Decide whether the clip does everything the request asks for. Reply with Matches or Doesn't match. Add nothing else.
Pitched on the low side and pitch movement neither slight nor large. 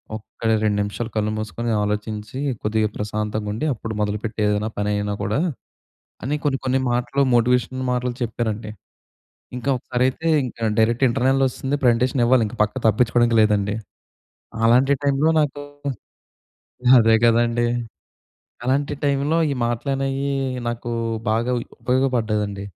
Matches